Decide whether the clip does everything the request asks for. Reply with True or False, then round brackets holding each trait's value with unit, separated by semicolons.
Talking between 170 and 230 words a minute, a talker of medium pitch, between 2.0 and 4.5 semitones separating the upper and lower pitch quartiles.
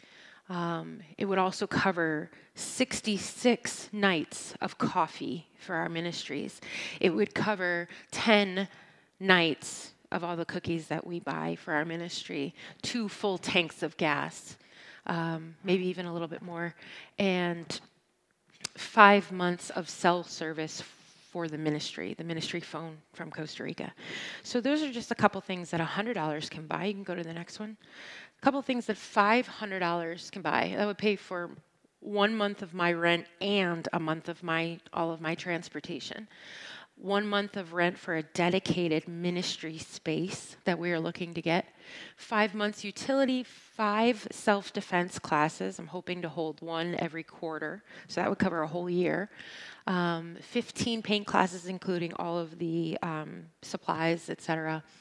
False (160 wpm; 175 Hz; 3.5 semitones)